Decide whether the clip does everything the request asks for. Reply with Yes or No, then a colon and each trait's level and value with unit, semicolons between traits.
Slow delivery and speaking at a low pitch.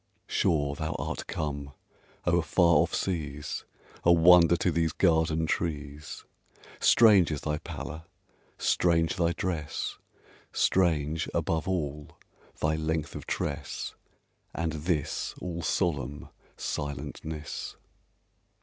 Yes: slow, 105 wpm; very low, 80 Hz